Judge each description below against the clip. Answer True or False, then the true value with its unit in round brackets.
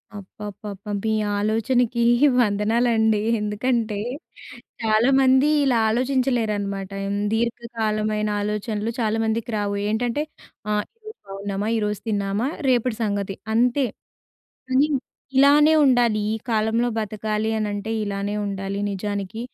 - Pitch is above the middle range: True (220 Hz)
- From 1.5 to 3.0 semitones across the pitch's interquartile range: True (2.6 semitones)